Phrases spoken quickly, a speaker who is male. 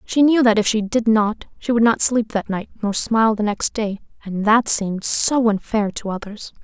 No: fast, 215 wpm; female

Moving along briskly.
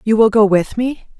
Yes: fast, 250 wpm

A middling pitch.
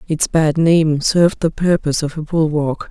Yes: medium, 160 Hz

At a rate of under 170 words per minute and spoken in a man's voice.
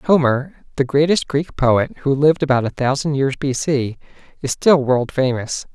No: average, 175 wpm; male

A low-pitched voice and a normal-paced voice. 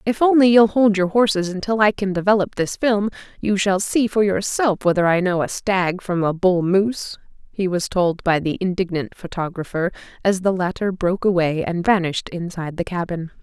No: high, 190 Hz; average, 190 wpm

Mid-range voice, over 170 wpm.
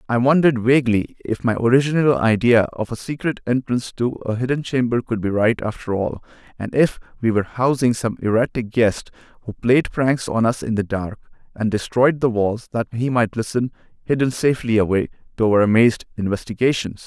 No: low, 120 Hz; average, 180 wpm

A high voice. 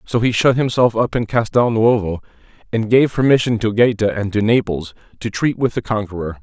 No: low, 110 Hz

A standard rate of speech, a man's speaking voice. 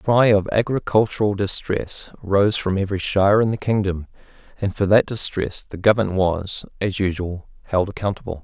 Yes: average, 165 wpm; male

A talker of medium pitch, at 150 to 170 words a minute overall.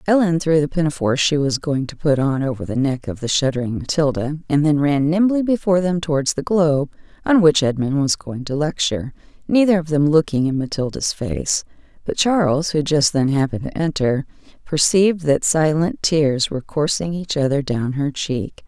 No: medium, 150 Hz; average, 190 wpm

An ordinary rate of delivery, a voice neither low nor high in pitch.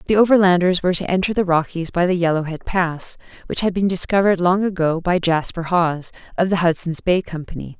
Yes: average, 190 wpm; medium, 175 Hz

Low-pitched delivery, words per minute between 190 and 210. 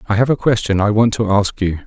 No: low, 105 Hz; fast, 290 wpm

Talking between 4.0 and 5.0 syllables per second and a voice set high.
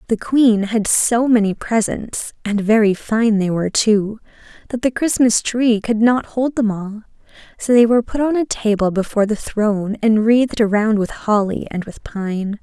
Yes: 4.6 syllables/s; high, 220 Hz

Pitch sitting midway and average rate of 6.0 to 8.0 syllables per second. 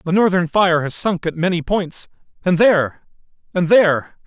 No: medium, 175 Hz; 5.0 syllables/s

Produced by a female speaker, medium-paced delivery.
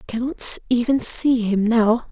Yes: female; average, 170 wpm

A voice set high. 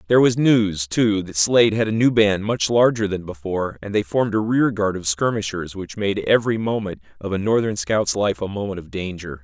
No: low, 100 Hz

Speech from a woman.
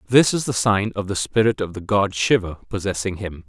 No: male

